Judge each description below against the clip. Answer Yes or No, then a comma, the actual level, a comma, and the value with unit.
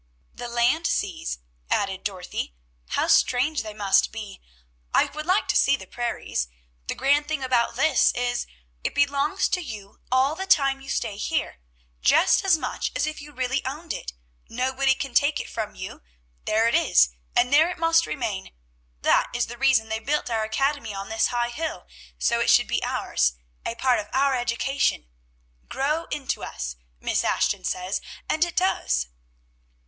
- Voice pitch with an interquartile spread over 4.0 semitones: Yes, average, 5.0 semitones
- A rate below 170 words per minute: No, average, 175 wpm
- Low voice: No, very high, 255 Hz